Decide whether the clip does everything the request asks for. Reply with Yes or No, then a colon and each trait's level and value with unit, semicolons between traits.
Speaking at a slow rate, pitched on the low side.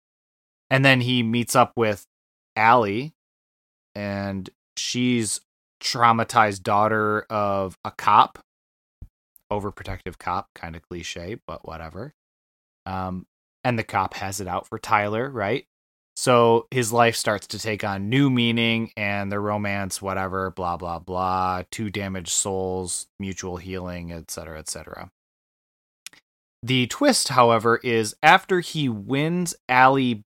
Yes: slow, 125 wpm; low, 100 Hz